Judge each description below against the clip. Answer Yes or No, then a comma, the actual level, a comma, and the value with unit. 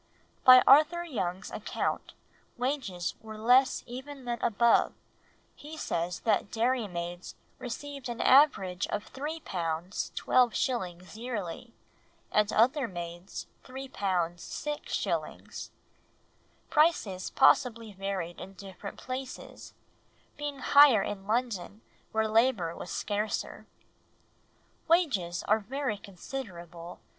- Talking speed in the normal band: No, slow, 95 wpm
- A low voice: No, high, 220 Hz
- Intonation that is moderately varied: No, wide, 6.0 semitones